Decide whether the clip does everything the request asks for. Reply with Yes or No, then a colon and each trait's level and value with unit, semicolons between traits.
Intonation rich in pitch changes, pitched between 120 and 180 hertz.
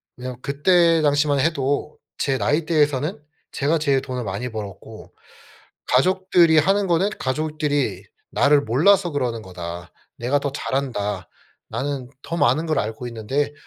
No: average, 4.0 semitones; medium, 140 Hz